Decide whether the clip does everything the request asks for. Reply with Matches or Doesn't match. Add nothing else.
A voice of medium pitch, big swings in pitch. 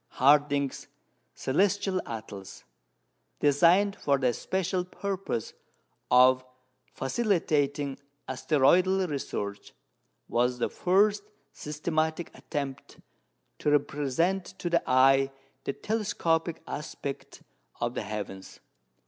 Matches